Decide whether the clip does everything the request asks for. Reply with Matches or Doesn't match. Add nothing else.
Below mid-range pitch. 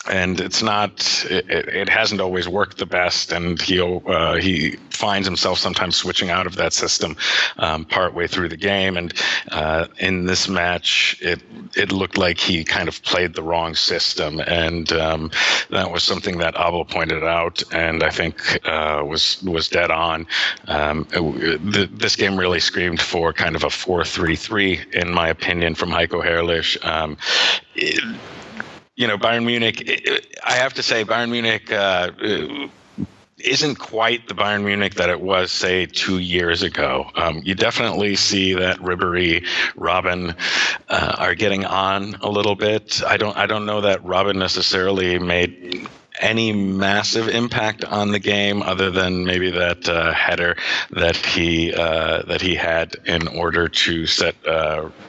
Matches